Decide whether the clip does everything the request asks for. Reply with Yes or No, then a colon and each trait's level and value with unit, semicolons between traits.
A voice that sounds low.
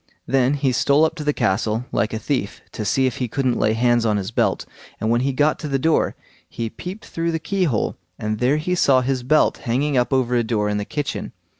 Yes: low, 130 Hz